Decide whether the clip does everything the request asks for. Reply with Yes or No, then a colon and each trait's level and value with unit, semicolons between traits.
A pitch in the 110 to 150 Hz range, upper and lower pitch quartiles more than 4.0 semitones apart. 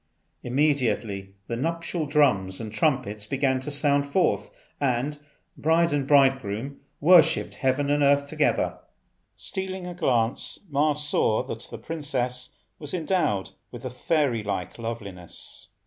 Yes: medium, 140 Hz; average, 4.4 semitones